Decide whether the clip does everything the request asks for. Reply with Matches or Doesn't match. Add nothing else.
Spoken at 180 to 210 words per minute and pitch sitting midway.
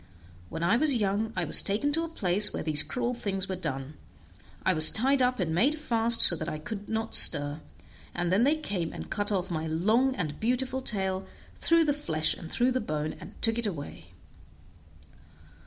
Doesn't match